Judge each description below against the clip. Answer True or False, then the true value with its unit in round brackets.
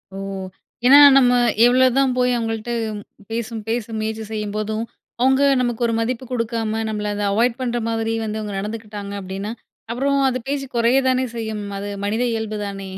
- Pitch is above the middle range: True (225 Hz)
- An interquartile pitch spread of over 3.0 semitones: False (2.6 semitones)